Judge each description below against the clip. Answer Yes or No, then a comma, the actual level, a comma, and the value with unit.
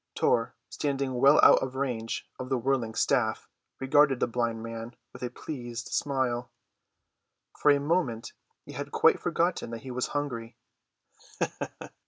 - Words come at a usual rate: Yes, average, 145 wpm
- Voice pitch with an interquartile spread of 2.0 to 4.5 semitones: Yes, average, 3.0 semitones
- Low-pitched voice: Yes, low, 125 Hz